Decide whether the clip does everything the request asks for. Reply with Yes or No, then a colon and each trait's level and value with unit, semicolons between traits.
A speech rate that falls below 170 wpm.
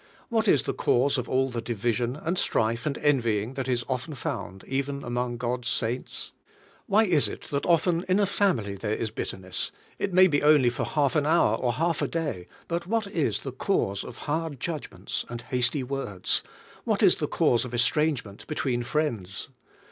No: average, 190 wpm